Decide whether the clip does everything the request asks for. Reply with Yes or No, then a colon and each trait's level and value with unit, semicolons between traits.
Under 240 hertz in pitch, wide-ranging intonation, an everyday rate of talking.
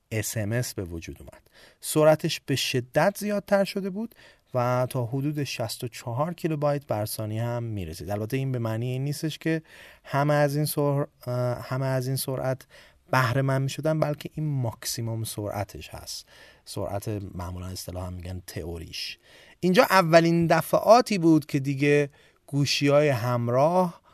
Yes: low, 135 Hz; wide, 5.8 semitones; average, 140 wpm